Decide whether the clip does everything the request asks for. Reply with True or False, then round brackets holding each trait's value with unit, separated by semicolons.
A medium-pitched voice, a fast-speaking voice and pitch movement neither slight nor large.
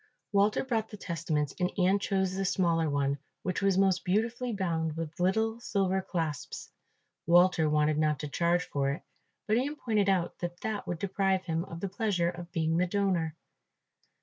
False (180 Hz; 175 wpm; 3.3 semitones)